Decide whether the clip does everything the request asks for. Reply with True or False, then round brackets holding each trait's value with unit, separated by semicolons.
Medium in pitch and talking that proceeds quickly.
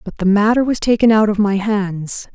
False (210 Hz; 230 wpm)